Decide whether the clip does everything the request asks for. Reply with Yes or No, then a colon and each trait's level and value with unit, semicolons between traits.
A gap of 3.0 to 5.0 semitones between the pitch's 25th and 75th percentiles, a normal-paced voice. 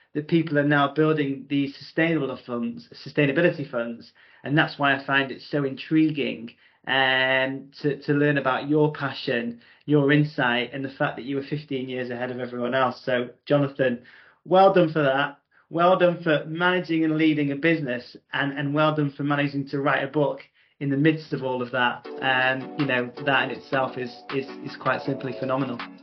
No: narrow, 2.5 semitones; average, 190 wpm